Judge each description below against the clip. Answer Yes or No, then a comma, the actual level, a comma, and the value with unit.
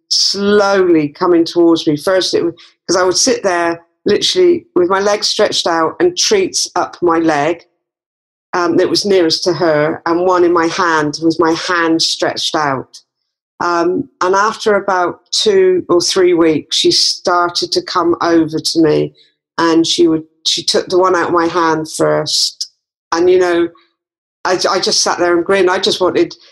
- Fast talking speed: No, average, 175 wpm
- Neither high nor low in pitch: Yes, medium, 175 Hz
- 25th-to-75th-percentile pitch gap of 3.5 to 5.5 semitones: No, average, 3.1 semitones